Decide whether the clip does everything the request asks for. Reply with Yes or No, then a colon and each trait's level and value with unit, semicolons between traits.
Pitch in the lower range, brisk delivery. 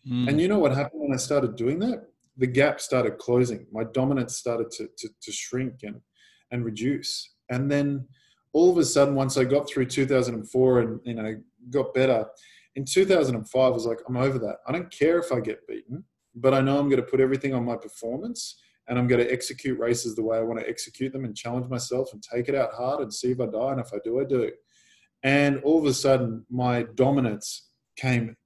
Yes: low, 130 Hz; fast, 230 wpm